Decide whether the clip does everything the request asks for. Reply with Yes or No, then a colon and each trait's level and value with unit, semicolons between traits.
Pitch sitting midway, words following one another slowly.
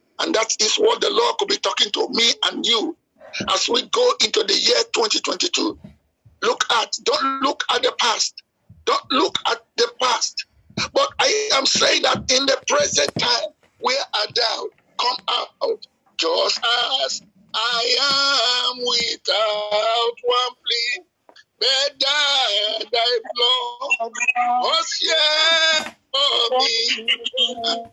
No: very high, 275 Hz; slow, 125 wpm